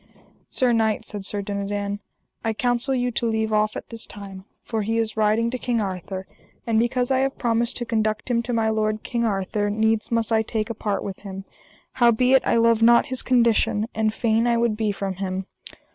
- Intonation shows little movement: Yes, narrow, 2.2 semitones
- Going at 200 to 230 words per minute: Yes, fast, 205 wpm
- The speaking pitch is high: Yes, high, 220 Hz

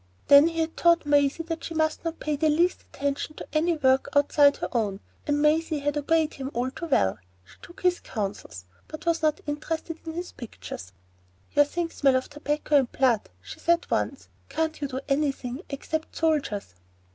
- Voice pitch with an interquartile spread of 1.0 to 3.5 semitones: Yes, average, 3.1 semitones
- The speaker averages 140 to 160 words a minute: No, average, 190 wpm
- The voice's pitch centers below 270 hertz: No, very high, 295 Hz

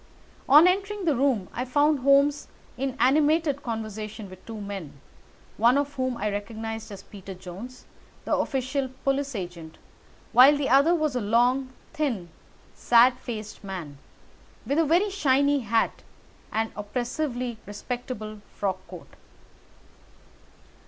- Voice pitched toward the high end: Yes, high, 245 Hz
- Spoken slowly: Yes, slow, 130 wpm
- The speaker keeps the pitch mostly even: No, average, 5.1 semitones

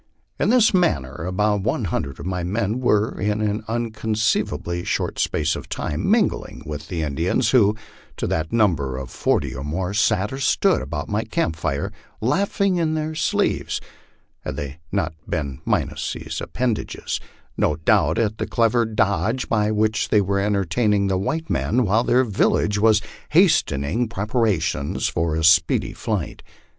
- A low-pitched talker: Yes, low, 105 Hz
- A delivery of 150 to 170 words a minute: Yes, average, 160 wpm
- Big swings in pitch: Yes, wide, 5.7 semitones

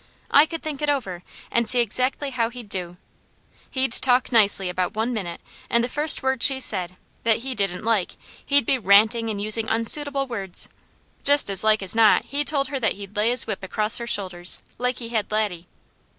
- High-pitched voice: Yes, high, 230 Hz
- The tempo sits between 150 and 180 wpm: No, average, 200 wpm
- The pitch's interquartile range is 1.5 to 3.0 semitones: No, average, 4.5 semitones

